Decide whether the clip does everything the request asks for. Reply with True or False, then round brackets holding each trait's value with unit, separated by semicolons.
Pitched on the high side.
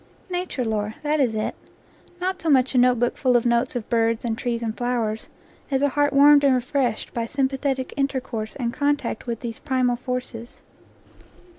True (250 Hz)